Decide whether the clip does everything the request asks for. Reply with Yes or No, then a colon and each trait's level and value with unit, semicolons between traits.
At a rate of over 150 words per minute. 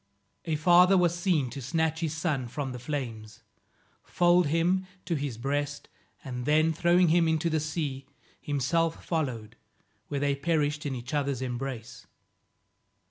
No: average, 145 wpm